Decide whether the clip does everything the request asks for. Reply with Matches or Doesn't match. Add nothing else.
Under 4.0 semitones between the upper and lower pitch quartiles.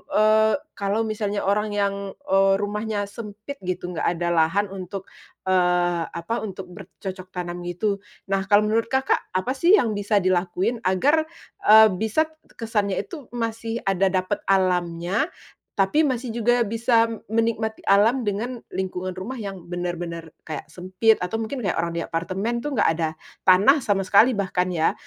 Matches